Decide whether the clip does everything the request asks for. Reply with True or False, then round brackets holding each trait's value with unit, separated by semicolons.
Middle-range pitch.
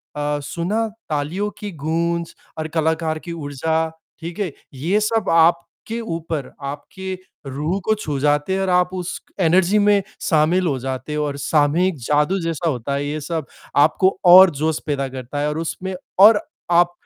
True (165 Hz)